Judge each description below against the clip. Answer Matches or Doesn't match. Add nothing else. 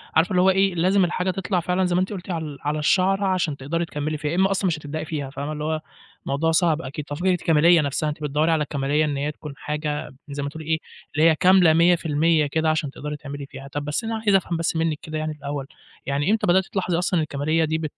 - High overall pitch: Doesn't match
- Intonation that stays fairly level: Doesn't match